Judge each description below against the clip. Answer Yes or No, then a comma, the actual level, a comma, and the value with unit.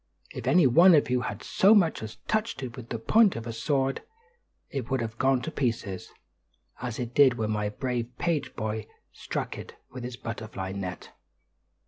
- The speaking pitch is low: Yes, low, 125 Hz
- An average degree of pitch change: Yes, average, 3.8 semitones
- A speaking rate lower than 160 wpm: No, average, 185 wpm